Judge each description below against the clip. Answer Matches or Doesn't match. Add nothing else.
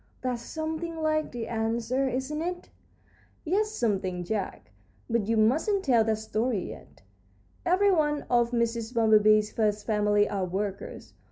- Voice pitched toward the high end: Matches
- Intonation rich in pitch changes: Matches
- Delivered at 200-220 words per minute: Doesn't match